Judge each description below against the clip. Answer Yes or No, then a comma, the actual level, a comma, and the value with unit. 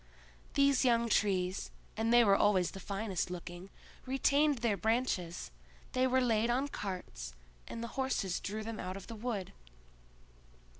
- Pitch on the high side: Yes, high, 220 Hz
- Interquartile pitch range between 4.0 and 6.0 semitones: Yes, average, 4.6 semitones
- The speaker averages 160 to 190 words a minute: No, average, 150 wpm